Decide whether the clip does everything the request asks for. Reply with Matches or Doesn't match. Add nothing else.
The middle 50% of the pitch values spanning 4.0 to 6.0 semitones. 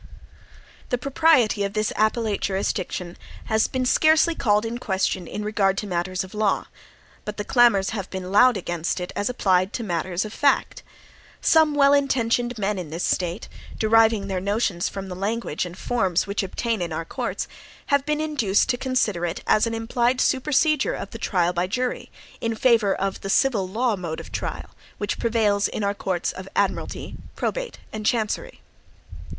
Matches